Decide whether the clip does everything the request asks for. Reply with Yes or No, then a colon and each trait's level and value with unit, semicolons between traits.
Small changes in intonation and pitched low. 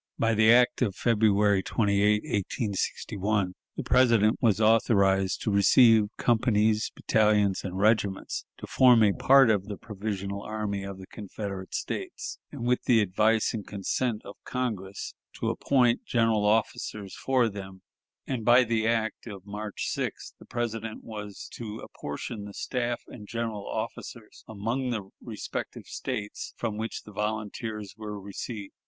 Yes: narrow, 2.3 semitones; low, 105 Hz